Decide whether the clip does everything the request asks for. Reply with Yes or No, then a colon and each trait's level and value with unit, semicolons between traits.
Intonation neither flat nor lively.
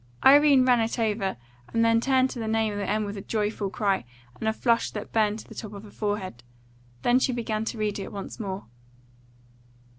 No: narrow, 2.2 semitones